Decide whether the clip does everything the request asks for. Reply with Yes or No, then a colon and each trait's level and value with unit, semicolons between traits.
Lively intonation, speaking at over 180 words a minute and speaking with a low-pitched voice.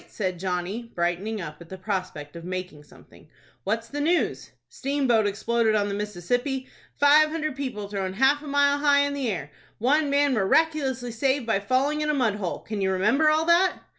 No: wide, 6.8 semitones; average, 190 wpm; high, 235 Hz